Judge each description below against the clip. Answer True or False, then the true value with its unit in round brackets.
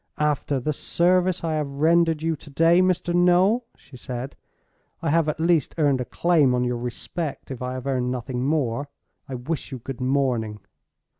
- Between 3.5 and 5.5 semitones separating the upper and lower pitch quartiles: True (4.7 semitones)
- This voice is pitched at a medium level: True (145 Hz)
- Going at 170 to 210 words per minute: True (180 wpm)